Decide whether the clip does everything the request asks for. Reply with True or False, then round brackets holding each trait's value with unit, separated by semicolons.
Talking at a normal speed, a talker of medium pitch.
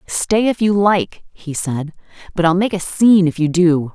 False (215 wpm; 180 Hz)